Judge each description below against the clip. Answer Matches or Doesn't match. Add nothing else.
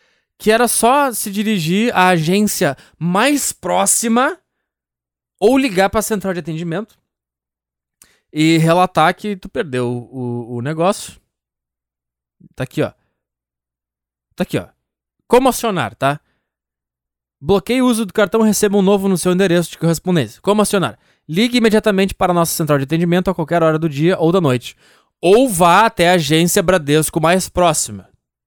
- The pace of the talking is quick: Doesn't match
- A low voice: Doesn't match